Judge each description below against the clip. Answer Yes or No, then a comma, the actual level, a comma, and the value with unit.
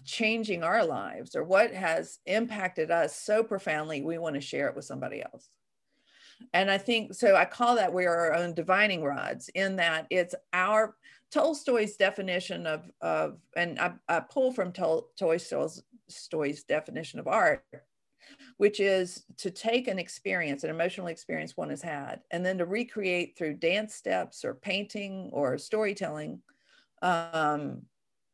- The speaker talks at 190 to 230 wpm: No, average, 155 wpm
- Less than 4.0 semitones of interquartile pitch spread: No, average, 4.3 semitones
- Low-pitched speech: No, medium, 185 Hz